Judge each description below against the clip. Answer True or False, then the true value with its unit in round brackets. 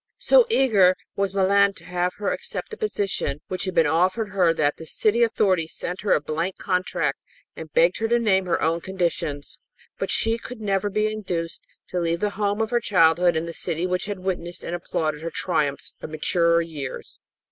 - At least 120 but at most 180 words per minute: False (200 wpm)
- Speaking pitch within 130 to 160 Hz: False (185 Hz)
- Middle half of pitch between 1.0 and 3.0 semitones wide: False (3.7 semitones)